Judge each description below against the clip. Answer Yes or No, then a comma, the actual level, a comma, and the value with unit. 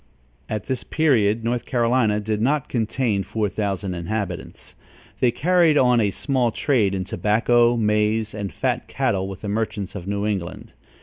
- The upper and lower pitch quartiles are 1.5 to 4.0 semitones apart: Yes, average, 3.1 semitones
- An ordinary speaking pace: Yes, average, 160 wpm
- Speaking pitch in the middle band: No, low, 110 Hz